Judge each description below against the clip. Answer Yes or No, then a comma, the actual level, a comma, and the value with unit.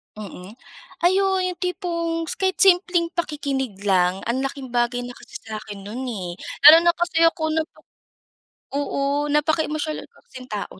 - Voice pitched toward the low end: No, very high, 290 Hz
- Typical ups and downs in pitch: No, wide, 6.0 semitones